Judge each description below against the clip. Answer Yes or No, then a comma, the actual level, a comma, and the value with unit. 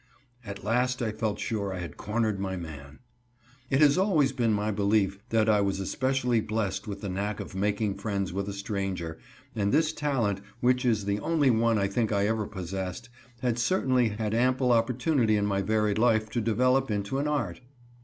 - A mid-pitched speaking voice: No, low, 110 Hz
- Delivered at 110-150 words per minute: No, average, 190 wpm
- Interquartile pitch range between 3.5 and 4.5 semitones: Yes, average, 3.8 semitones